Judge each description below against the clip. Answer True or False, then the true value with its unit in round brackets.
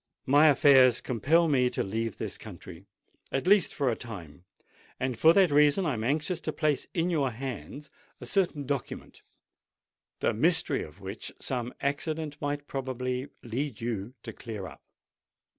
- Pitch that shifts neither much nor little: True (4.1 semitones)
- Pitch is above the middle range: False (135 Hz)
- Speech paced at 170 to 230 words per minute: False (155 wpm)